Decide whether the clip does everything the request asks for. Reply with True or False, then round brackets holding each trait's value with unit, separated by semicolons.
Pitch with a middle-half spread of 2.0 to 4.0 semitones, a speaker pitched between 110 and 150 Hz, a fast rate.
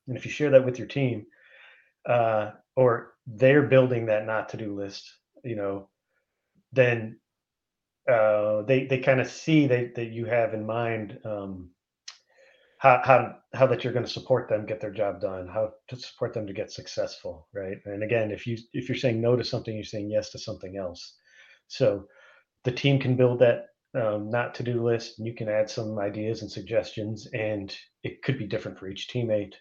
False (2.9 semitones; 115 Hz; 195 wpm)